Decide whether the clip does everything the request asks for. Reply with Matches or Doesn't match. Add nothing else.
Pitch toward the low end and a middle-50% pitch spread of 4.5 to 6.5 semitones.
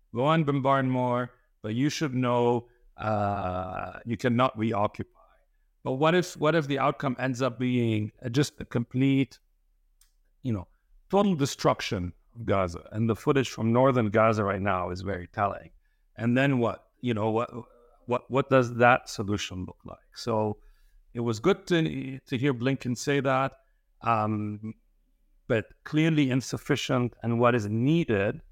Doesn't match